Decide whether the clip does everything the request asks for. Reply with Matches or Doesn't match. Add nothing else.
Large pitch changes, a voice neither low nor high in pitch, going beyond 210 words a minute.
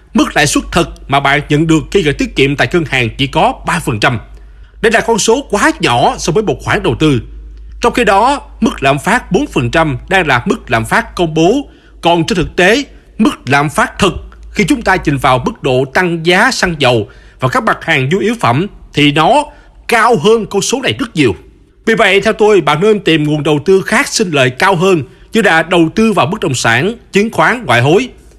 Matches